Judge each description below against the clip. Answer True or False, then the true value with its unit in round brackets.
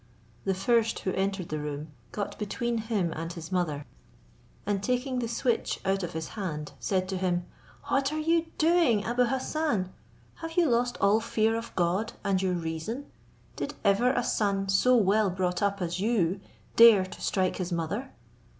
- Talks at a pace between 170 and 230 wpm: True (175 wpm)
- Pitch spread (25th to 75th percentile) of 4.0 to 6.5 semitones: True (4.7 semitones)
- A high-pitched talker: True (200 Hz)